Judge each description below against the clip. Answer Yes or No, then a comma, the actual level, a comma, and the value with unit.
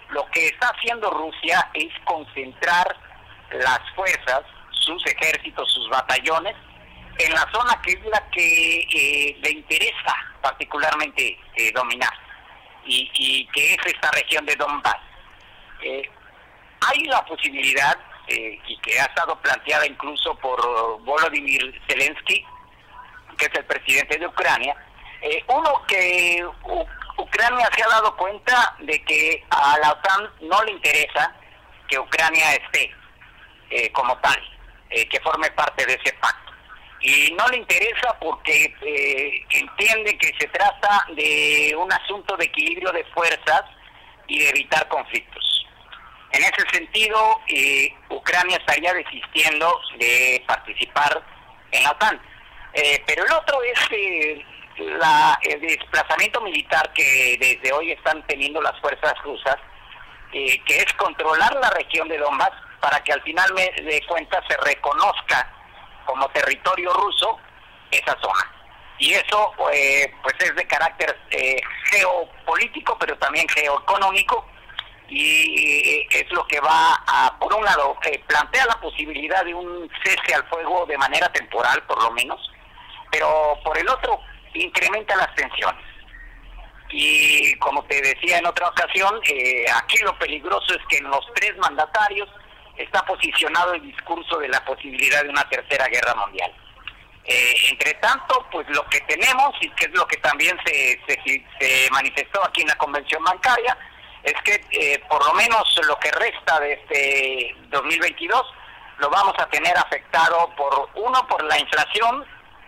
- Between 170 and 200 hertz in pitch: Yes, high, 190 Hz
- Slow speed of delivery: No, average, 145 wpm